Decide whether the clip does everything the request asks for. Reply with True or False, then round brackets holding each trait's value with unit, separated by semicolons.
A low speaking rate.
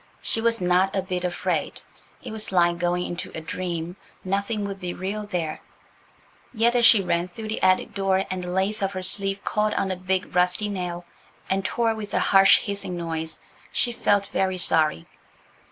False (185 wpm)